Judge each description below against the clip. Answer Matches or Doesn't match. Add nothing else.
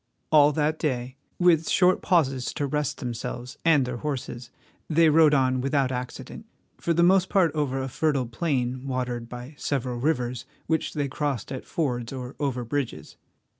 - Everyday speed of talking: Matches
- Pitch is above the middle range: Doesn't match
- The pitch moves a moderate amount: Matches